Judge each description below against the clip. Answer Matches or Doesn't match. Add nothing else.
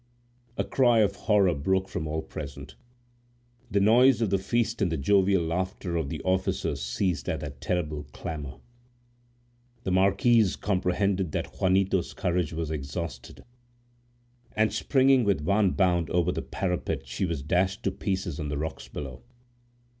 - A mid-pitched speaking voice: Doesn't match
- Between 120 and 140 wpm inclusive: Doesn't match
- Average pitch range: Matches